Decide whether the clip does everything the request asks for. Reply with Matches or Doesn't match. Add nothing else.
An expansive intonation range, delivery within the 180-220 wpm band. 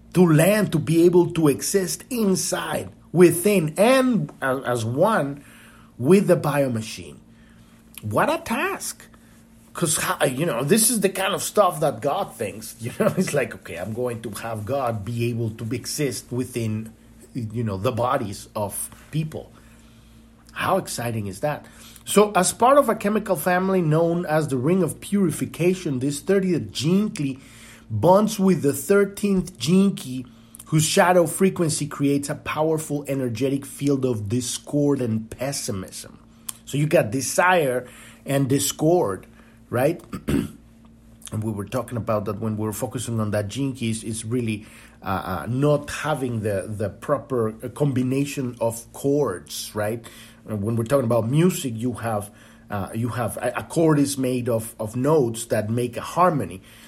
Doesn't match